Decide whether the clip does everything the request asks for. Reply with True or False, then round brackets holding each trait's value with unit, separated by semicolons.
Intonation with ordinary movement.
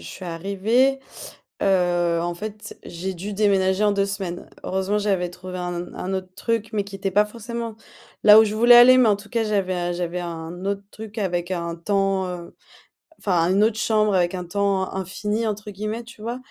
True (3.0 semitones)